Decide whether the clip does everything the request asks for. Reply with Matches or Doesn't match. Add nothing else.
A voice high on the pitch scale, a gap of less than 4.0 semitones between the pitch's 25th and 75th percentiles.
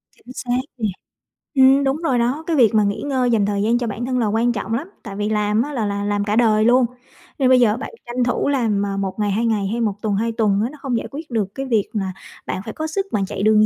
Matches